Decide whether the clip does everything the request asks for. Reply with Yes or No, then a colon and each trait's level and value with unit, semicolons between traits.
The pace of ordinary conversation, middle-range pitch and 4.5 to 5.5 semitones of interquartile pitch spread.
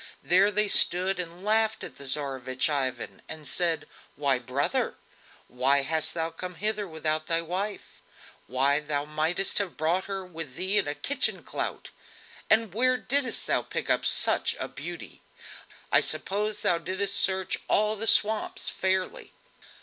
Yes: average, 155 wpm; medium, 180 Hz; average, 5.1 semitones